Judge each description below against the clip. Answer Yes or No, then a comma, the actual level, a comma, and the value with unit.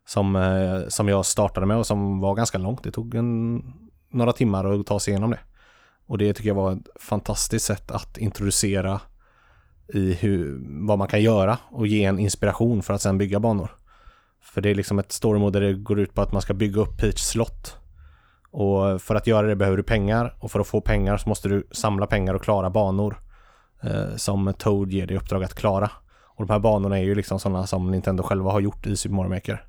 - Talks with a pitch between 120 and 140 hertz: No, low, 100 Hz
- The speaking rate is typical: No, fast, 220 wpm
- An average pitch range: No, narrow, 1.8 semitones